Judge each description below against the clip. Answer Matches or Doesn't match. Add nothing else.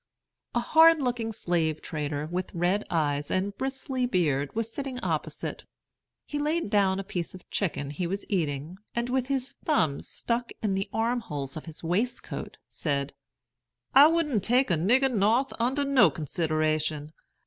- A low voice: Doesn't match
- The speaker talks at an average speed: Matches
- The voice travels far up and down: Matches